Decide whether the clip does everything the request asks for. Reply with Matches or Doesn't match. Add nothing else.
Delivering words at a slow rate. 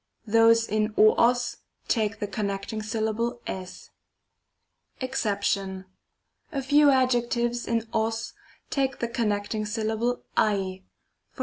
Matches